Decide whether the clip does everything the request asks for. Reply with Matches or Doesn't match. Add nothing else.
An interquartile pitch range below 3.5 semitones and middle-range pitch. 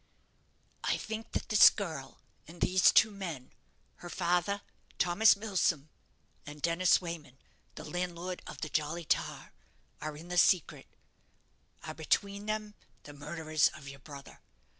Doesn't match